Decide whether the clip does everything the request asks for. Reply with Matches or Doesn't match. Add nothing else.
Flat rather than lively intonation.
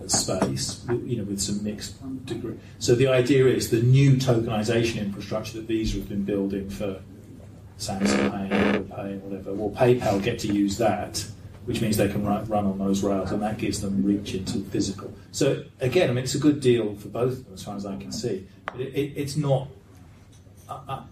Doesn't match